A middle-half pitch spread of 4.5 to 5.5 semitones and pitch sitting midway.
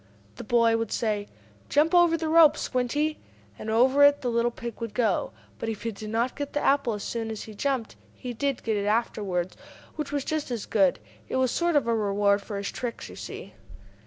No: average, 4.8 semitones; high, 235 Hz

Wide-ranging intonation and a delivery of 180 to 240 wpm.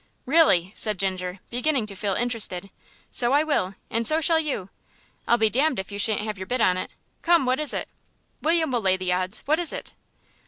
Yes: wide, 7.4 semitones; average, 200 wpm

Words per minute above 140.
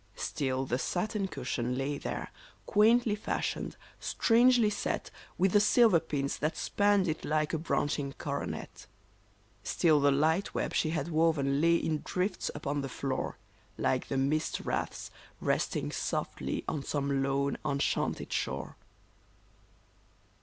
No: slow, 135 wpm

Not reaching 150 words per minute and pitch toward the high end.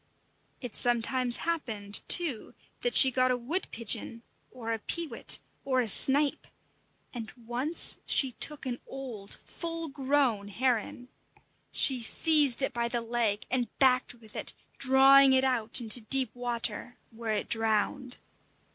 Yes: average, 140 wpm; high, 245 Hz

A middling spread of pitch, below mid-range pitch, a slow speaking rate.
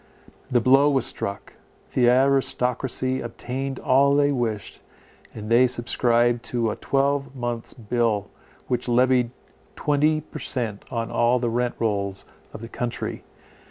No: narrow, 2.3 semitones; low, 125 Hz; slow, 130 wpm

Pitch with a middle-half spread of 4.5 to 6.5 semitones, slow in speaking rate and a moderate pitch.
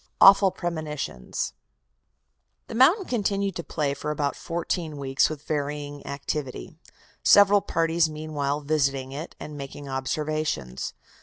No: average, 3.3 semitones; slow, 120 wpm; medium, 150 Hz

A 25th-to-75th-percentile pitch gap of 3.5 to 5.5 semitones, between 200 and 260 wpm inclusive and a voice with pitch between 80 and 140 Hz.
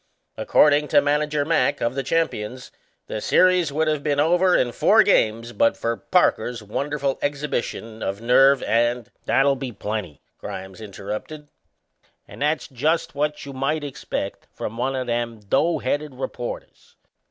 No: average, 4.4 semitones; average, 155 wpm; low, 135 Hz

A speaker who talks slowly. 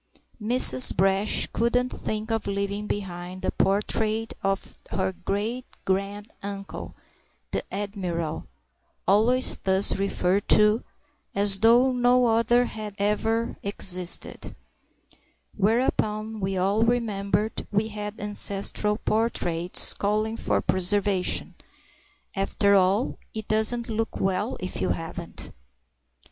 Yes: slow, 105 wpm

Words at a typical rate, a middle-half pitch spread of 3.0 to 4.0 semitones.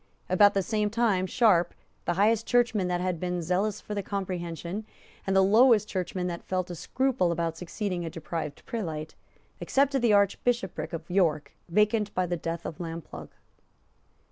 Yes: average, 165 wpm; average, 3.7 semitones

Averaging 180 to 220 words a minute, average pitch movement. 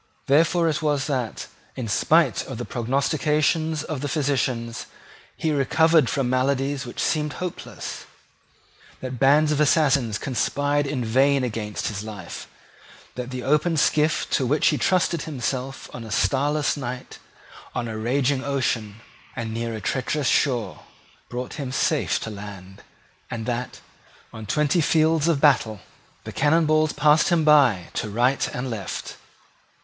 No: average, 145 wpm; average, 4.1 semitones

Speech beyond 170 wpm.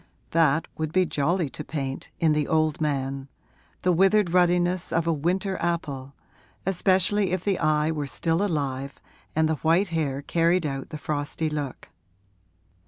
No: average, 155 wpm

